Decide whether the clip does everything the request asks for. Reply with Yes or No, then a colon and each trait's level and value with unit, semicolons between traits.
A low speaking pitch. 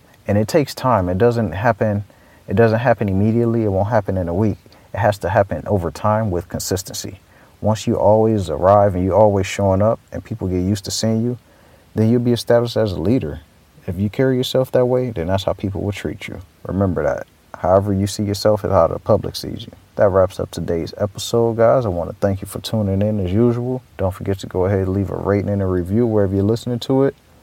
Yes: low, 105 Hz